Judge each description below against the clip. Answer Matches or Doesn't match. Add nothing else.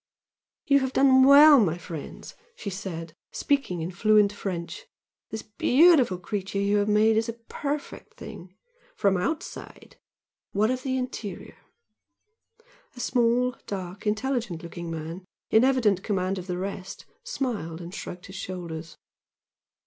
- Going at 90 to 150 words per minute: Matches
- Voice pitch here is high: Matches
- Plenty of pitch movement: Matches